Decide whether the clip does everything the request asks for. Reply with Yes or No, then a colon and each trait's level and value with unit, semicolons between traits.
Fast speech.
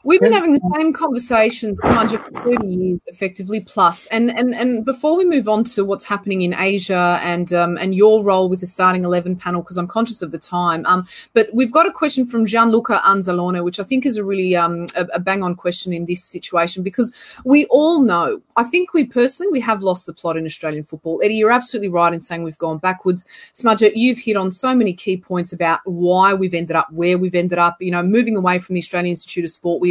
Yes: fast, 235 wpm